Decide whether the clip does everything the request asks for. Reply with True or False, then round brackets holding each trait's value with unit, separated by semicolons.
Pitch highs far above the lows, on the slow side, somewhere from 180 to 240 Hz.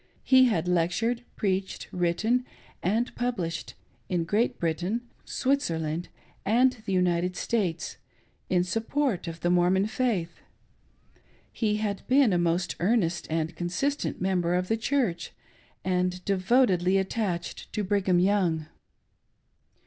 False (4.4 semitones; 120 wpm; 185 Hz)